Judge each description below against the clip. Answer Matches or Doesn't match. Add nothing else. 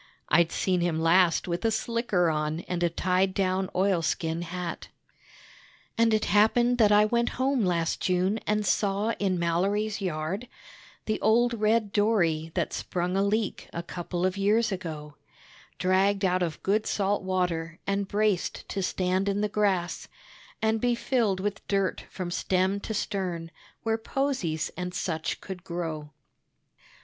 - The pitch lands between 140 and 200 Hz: Matches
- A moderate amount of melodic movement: Matches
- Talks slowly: Doesn't match